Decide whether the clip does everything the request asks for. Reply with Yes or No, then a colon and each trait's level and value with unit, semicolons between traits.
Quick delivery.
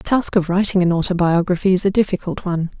Yes: fast, 215 wpm